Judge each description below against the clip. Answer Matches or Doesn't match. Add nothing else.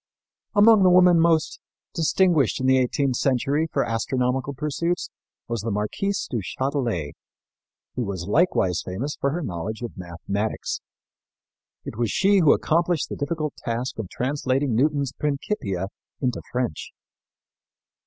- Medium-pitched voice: Doesn't match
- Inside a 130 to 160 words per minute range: Matches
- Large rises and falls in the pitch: Matches